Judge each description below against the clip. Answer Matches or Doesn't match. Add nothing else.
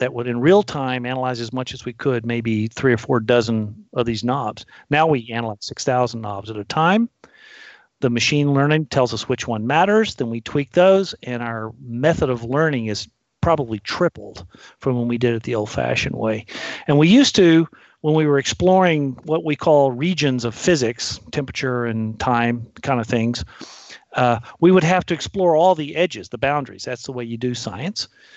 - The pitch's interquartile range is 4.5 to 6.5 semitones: Matches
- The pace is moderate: Matches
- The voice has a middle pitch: Doesn't match